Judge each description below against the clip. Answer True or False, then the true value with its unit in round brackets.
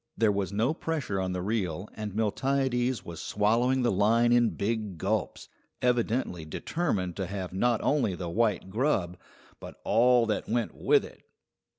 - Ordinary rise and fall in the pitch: True (4.3 semitones)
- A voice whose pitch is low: True (110 Hz)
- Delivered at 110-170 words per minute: True (160 wpm)